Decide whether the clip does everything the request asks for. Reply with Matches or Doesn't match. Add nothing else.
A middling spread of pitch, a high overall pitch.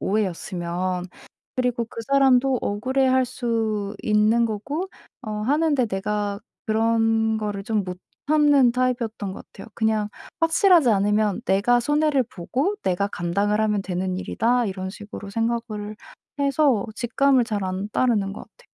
Matches